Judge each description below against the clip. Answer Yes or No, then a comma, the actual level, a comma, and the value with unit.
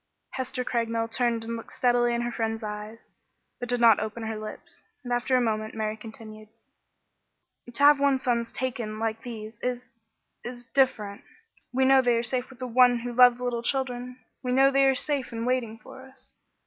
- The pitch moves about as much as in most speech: No, narrow, 2.1 semitones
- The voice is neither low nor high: No, high, 240 Hz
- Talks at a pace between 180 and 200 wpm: Yes, average, 190 wpm